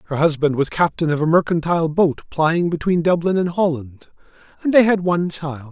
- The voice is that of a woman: No, male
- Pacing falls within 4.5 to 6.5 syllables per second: Yes, 5.5 syllables/s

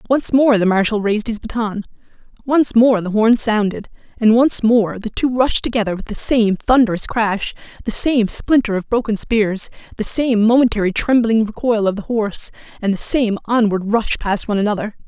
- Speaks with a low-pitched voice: No, high, 220 Hz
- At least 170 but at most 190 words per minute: Yes, average, 185 wpm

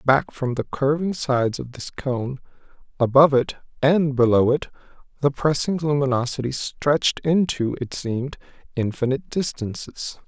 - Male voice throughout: Yes, male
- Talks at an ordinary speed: No, slow, 130 wpm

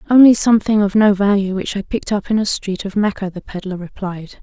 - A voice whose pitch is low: No, high, 200 Hz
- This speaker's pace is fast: Yes, fast, 230 wpm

